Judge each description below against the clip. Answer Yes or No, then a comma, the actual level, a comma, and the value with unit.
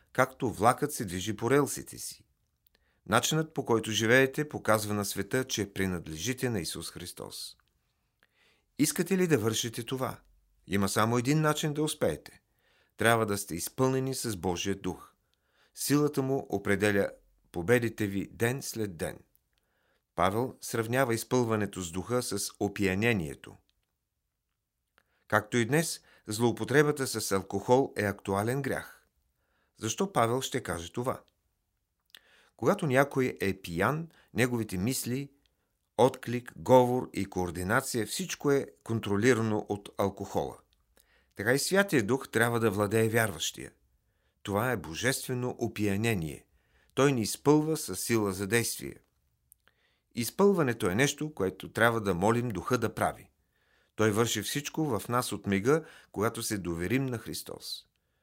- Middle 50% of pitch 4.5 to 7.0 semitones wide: Yes, average, 4.9 semitones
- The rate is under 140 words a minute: Yes, average, 125 wpm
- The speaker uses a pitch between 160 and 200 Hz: No, low, 115 Hz